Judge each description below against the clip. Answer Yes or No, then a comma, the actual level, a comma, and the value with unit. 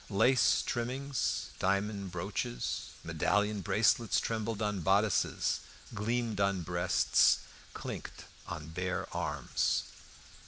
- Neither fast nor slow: No, slow, 90 wpm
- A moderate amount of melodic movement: Yes, average, 3.6 semitones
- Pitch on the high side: No, low, 100 Hz